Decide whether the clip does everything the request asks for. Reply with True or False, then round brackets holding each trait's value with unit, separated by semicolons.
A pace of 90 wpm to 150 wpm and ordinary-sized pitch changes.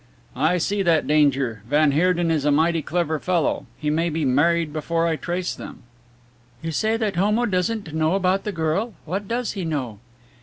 False (185 wpm; 3.4 semitones)